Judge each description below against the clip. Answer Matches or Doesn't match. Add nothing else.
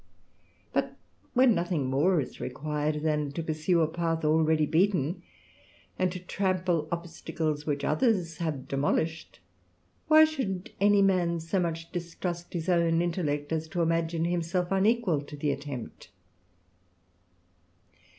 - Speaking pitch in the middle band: Matches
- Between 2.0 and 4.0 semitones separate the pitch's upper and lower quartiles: Matches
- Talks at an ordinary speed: Doesn't match